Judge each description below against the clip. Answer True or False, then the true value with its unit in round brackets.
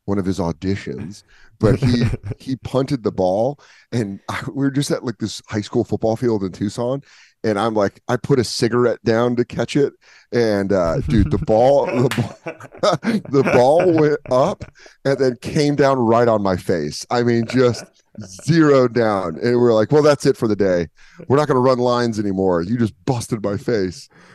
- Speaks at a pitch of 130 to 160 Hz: False (120 Hz)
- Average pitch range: True (4.0 semitones)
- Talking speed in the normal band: True (190 wpm)